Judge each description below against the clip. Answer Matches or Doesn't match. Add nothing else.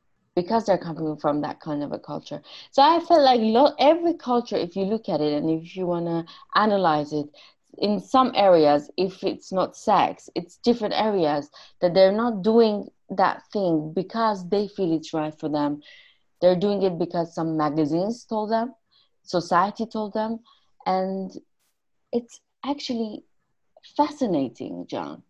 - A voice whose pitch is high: Matches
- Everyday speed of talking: Matches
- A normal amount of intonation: Doesn't match